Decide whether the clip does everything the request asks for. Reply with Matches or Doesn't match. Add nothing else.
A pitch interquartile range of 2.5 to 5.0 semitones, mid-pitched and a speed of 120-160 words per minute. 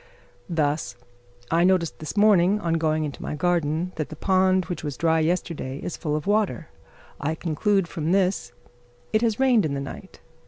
Doesn't match